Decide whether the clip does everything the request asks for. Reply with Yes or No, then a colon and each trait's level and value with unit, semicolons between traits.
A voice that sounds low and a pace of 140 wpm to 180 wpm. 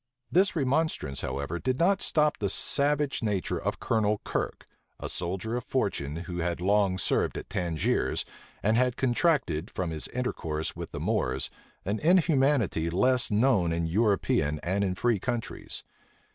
Yes: low, 105 Hz; average, 150 wpm